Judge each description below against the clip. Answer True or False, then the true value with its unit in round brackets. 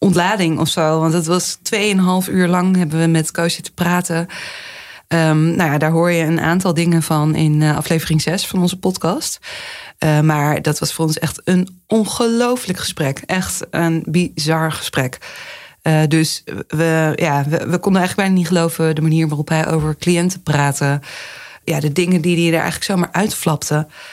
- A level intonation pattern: True (2.3 semitones)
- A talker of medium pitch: True (165 Hz)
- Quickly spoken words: False (180 wpm)